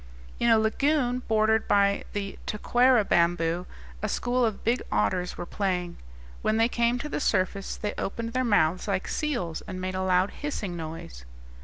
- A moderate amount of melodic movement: Yes, average, 4.6 semitones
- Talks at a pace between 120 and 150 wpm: No, average, 170 wpm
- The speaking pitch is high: Yes, high, 205 Hz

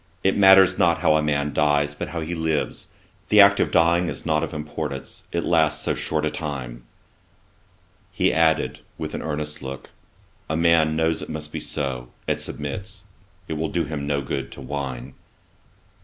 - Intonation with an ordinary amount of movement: No, narrow, 2.3 semitones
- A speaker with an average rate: Yes, average, 180 wpm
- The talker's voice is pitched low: Yes, very low, 80 Hz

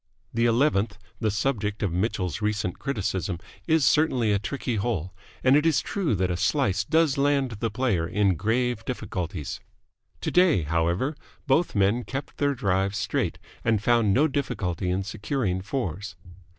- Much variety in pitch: Yes, wide, 5.9 semitones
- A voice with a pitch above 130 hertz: No, low, 110 Hz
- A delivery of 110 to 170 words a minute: Yes, average, 150 wpm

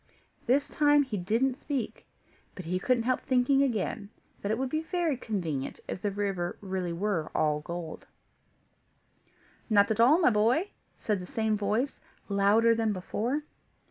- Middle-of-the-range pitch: No, high, 220 Hz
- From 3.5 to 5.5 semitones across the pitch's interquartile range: Yes, average, 5.0 semitones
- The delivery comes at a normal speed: Yes, average, 155 wpm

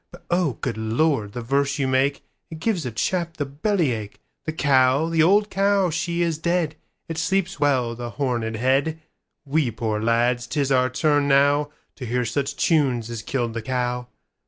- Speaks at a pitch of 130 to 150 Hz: Yes, medium, 140 Hz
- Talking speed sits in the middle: Yes, average, 160 wpm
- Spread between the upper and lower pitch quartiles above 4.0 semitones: Yes, average, 4.8 semitones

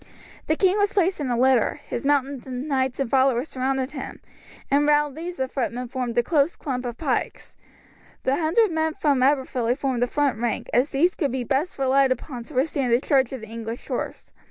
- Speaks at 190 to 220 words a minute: Yes, fast, 205 wpm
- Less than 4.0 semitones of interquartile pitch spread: Yes, average, 2.9 semitones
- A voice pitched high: Yes, very high, 270 Hz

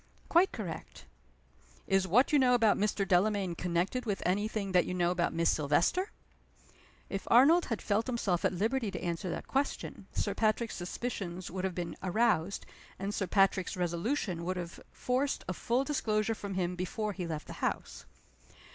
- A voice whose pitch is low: No, high, 195 Hz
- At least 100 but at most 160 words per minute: No, average, 175 wpm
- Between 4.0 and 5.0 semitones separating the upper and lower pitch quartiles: Yes, average, 4.3 semitones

